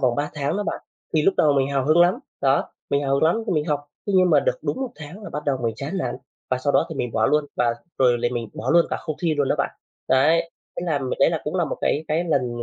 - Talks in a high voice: No, medium, 145 Hz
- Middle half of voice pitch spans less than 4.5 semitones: Yes, average, 3.9 semitones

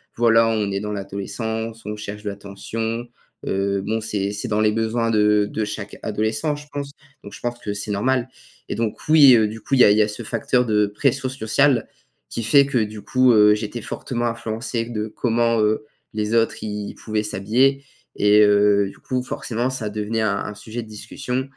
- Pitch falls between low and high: No, low, 110 Hz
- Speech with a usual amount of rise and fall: No, narrow, 2.3 semitones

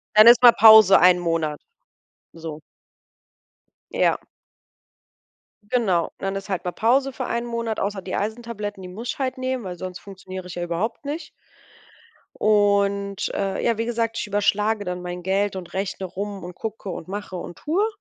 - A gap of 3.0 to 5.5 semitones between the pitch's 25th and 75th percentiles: Yes, average, 3.6 semitones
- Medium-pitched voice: No, high, 200 Hz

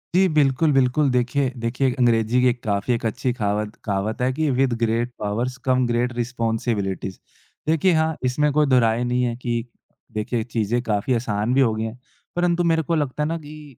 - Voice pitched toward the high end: No, low, 125 Hz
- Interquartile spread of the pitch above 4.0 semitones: No, average, 3.4 semitones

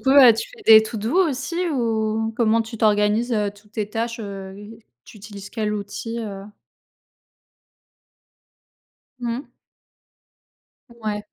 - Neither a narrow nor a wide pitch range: No, narrow, 2.2 semitones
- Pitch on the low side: No, high, 220 Hz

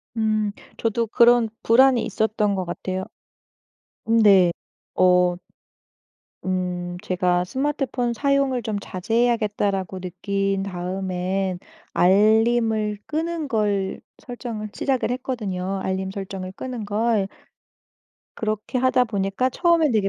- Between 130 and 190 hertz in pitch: No, high, 210 Hz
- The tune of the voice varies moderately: Yes, average, 4.1 semitones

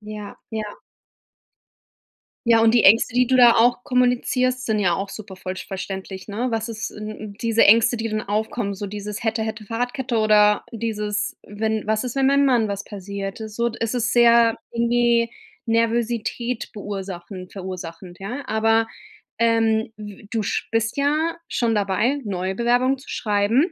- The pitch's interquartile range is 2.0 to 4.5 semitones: Yes, narrow, 2.5 semitones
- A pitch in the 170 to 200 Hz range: No, high, 220 Hz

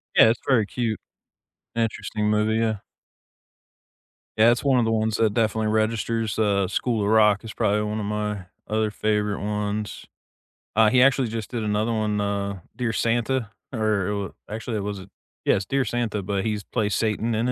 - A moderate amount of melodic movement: No, narrow, 1.6 semitones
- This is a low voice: Yes, low, 110 Hz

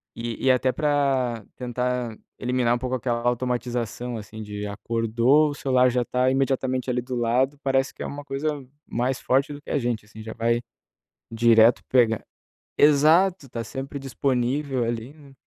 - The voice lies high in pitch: No, low, 125 Hz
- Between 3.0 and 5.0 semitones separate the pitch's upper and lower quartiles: No, narrow, 2.4 semitones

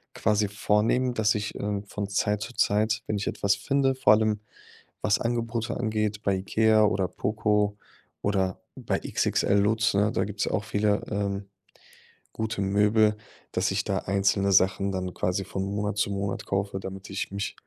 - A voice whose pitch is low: Yes, low, 105 Hz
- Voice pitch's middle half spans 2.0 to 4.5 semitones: No, narrow, 1.6 semitones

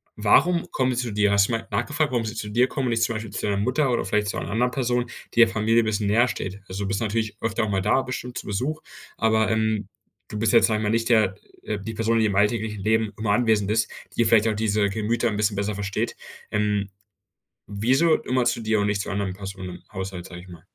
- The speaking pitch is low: Yes, low, 110 Hz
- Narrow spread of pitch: Yes, narrow, 2.3 semitones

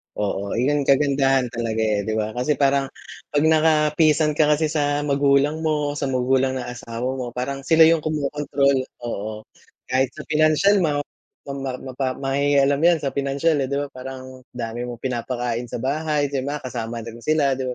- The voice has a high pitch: No, low, 135 Hz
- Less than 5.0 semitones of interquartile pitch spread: Yes, average, 3.0 semitones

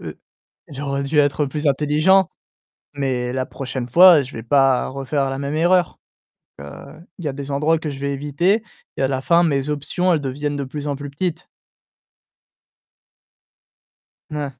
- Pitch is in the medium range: Yes, medium, 145 Hz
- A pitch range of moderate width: No, narrow, 2.3 semitones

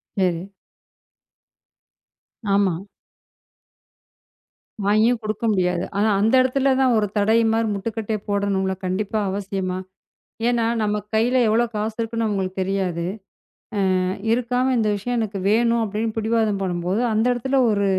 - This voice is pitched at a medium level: No, high, 215 Hz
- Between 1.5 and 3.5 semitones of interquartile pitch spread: Yes, average, 2.8 semitones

